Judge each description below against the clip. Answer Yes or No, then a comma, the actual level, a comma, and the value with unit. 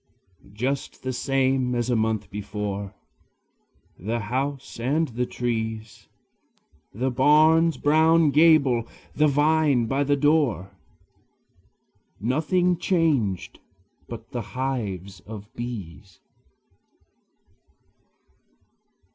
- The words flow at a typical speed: No, slow, 90 wpm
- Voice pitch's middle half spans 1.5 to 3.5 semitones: No, average, 5.1 semitones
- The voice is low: Yes, low, 125 Hz